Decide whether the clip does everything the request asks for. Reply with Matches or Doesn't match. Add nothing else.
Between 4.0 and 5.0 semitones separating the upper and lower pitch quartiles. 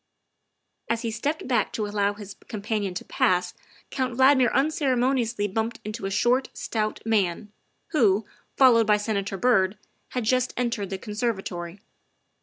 Doesn't match